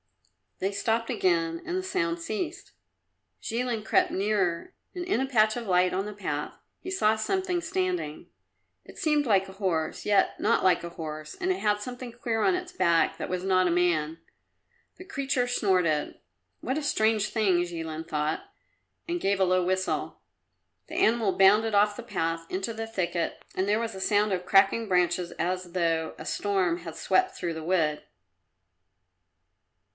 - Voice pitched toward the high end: Yes, high, 195 Hz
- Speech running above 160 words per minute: Yes, average, 170 wpm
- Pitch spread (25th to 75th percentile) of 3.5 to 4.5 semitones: No, average, 5.1 semitones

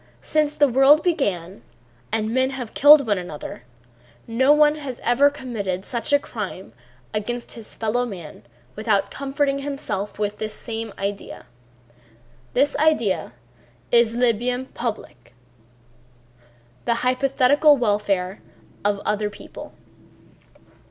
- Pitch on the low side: No, high, 235 Hz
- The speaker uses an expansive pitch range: No, average, 5.0 semitones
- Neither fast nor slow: No, slow, 120 wpm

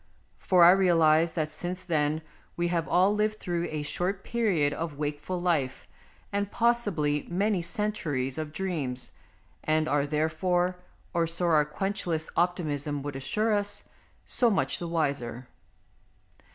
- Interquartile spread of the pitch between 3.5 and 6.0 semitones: Yes, average, 3.8 semitones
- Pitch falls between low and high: Yes, medium, 170 Hz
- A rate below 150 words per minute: Yes, average, 140 wpm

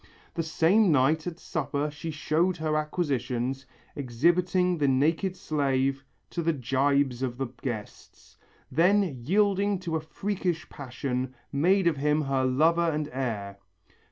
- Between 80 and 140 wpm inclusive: Yes, slow, 135 wpm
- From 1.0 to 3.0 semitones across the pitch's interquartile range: No, average, 4.3 semitones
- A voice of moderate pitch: Yes, medium, 150 Hz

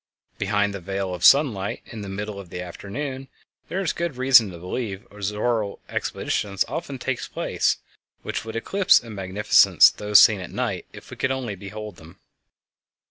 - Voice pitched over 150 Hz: No, low, 105 Hz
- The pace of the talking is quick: No, average, 165 wpm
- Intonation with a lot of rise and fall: No, average, 4.5 semitones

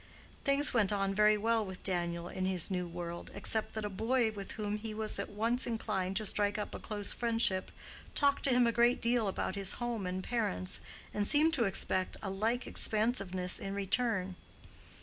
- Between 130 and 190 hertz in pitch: No, high, 210 Hz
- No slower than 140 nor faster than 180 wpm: No, average, 190 wpm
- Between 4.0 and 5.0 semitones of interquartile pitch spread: No, average, 3.6 semitones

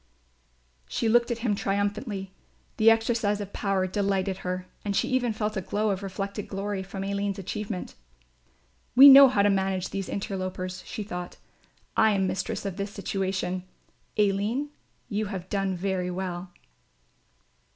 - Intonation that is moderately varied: No, narrow, 1.9 semitones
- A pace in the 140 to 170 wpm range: Yes, average, 150 wpm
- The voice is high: Yes, high, 200 Hz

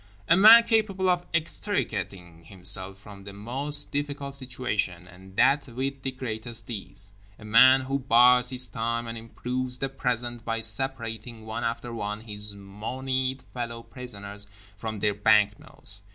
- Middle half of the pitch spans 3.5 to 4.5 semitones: Yes, average, 4.2 semitones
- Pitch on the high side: No, low, 115 Hz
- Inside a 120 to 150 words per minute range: Yes, average, 145 wpm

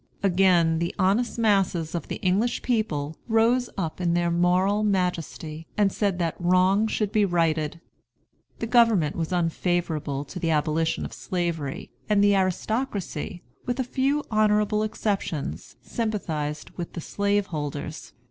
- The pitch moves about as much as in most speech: Yes, average, 4.4 semitones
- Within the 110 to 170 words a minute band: Yes, average, 140 wpm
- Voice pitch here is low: No, medium, 185 Hz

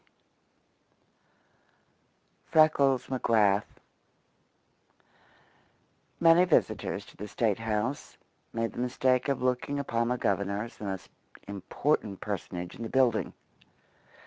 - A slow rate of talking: Yes, slow, 105 wpm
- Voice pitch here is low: Yes, low, 115 Hz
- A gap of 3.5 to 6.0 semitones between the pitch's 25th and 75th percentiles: Yes, average, 4.3 semitones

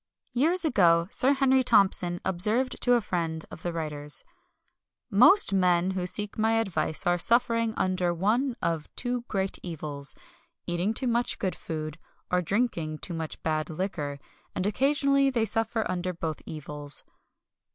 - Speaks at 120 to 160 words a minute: Yes, average, 150 wpm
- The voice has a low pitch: No, medium, 185 Hz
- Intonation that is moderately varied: No, wide, 6.0 semitones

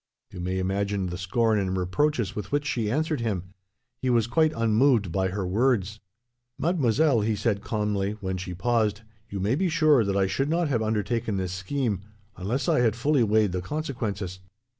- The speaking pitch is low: Yes, low, 110 Hz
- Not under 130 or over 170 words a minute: No, average, 185 wpm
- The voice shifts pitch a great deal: No, average, 4.9 semitones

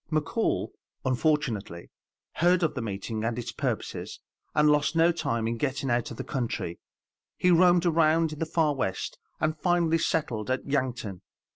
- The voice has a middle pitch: Yes, medium, 145 Hz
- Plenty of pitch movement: Yes, wide, 5.8 semitones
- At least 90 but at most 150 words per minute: No, average, 160 wpm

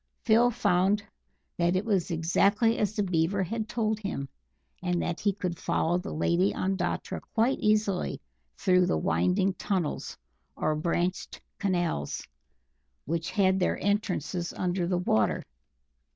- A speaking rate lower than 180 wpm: Yes, slow, 135 wpm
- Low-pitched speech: No, medium, 185 Hz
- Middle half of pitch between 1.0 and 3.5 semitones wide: Yes, average, 3.1 semitones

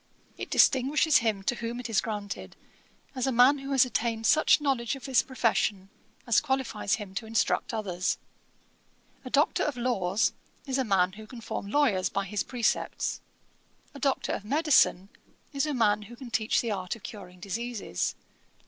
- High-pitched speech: Yes, high, 230 Hz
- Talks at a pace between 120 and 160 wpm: No, average, 175 wpm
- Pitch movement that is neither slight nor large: Yes, average, 4.5 semitones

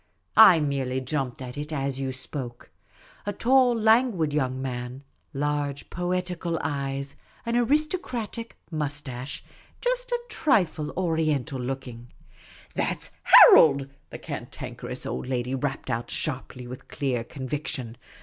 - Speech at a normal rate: No, slow, 130 wpm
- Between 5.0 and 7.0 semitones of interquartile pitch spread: Yes, wide, 5.5 semitones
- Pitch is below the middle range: No, medium, 145 Hz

